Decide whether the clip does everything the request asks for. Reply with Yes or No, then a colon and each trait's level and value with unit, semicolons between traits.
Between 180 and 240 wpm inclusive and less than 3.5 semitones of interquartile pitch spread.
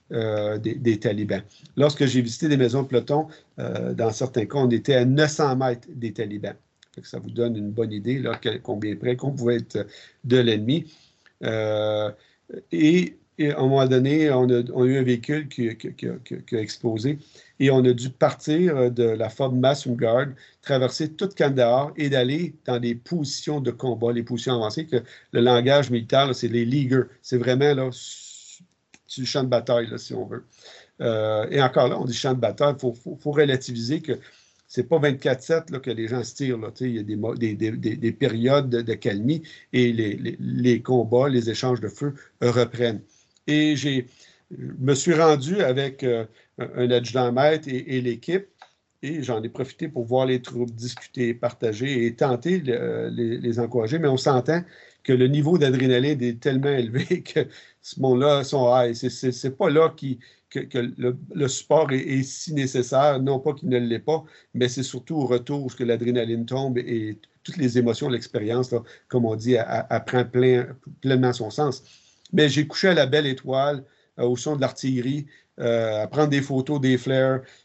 Yes: average, 195 wpm; average, 3.1 semitones